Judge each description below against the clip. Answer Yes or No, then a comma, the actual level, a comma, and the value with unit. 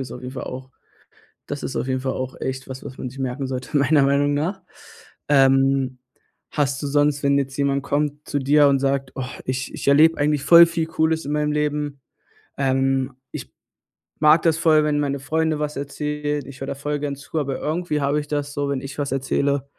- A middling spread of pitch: No, narrow, 1.7 semitones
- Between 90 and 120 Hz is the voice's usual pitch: No, medium, 140 Hz